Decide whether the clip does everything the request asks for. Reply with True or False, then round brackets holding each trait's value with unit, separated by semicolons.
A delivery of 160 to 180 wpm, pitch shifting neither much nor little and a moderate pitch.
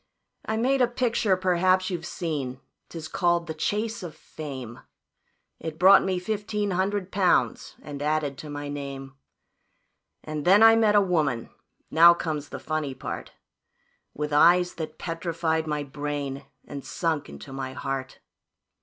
False (145 wpm; 4.3 semitones; 160 Hz)